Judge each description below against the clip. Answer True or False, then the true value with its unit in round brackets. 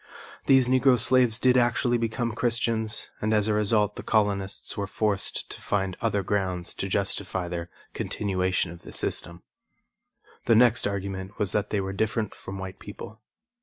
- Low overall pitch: True (105 Hz)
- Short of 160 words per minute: False (165 wpm)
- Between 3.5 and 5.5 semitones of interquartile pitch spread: False (3.1 semitones)